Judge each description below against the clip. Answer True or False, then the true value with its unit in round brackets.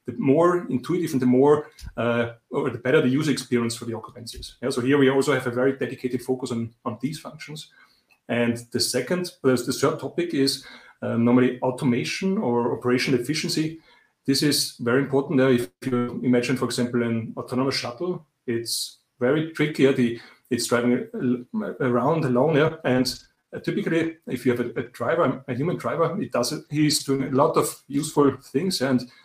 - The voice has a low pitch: True (130 Hz)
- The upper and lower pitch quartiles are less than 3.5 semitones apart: True (3.1 semitones)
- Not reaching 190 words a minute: True (180 wpm)